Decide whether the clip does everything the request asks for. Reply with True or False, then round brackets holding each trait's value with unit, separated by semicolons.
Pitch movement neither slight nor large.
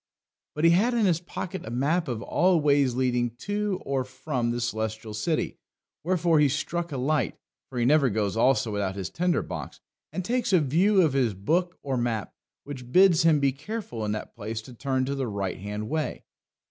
False (6.4 semitones)